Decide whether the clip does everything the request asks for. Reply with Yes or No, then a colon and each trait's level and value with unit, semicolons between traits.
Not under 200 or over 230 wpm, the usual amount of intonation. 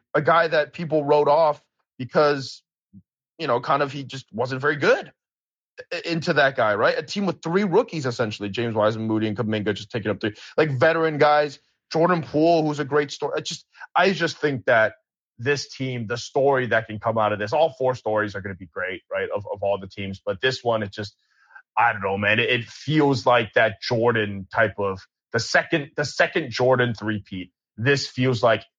No: fast, 205 wpm; wide, 5.7 semitones